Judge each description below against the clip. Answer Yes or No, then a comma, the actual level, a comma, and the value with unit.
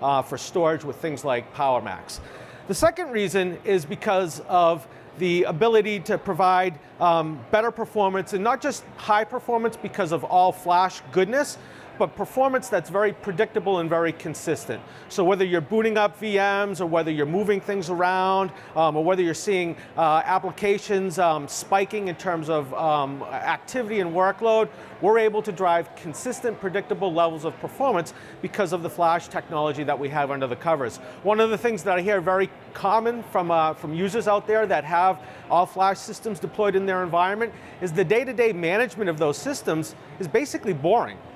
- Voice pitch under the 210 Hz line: Yes, high, 190 Hz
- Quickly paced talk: No, average, 175 wpm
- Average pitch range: Yes, average, 4.0 semitones